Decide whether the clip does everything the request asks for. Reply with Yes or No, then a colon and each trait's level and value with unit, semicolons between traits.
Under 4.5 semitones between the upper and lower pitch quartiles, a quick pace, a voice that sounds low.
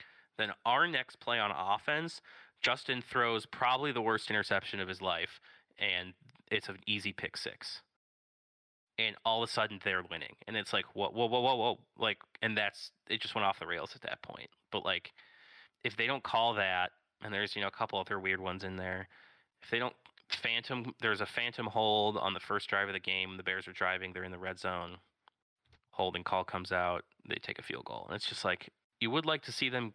Yes: average, 3.5 semitones; fast, 220 wpm; low, 100 Hz